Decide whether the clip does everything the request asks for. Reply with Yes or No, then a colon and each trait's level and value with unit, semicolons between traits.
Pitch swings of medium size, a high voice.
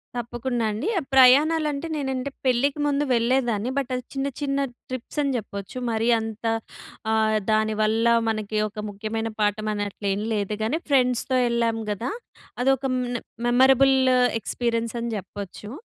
Yes: average, 3.6 semitones; high, 235 Hz